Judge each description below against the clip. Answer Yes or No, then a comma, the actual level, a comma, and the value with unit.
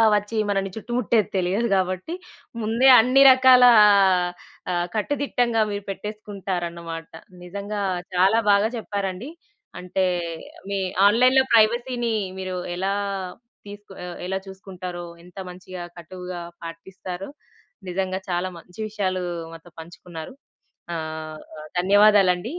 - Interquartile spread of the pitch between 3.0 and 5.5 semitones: Yes, average, 3.3 semitones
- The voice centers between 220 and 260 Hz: No, high, 195 Hz